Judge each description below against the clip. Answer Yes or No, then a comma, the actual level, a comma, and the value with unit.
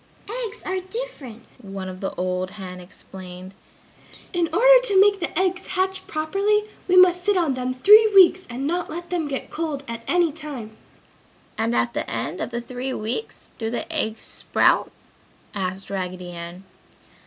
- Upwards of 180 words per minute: No, average, 160 wpm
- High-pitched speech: Yes, very high, 285 Hz